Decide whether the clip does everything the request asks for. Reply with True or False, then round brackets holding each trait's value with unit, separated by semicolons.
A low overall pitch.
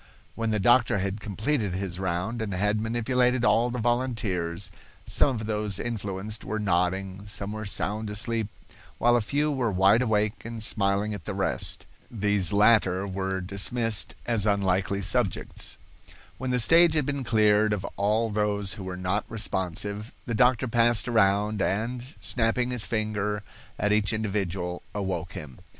True (105 Hz)